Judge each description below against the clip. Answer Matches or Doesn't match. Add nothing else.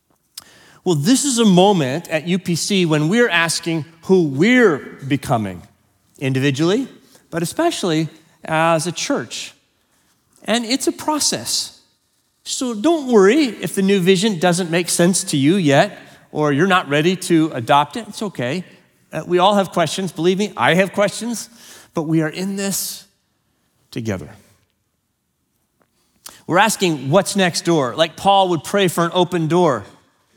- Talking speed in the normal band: Matches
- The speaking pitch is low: Doesn't match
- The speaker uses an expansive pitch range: Doesn't match